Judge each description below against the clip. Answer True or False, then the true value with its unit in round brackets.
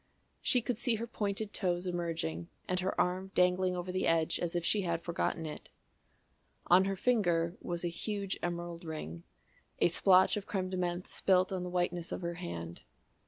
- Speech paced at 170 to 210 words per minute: True (185 wpm)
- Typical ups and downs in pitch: False (1.8 semitones)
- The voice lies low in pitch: False (180 Hz)